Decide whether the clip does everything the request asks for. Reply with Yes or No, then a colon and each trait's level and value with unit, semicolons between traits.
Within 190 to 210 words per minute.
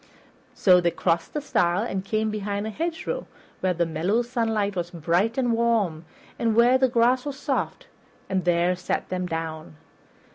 No: average, 170 wpm